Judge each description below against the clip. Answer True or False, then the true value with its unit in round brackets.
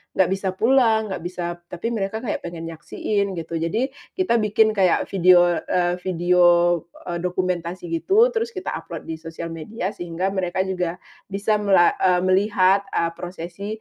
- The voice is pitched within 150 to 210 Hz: True (185 Hz)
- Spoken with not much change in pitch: False (3.2 semitones)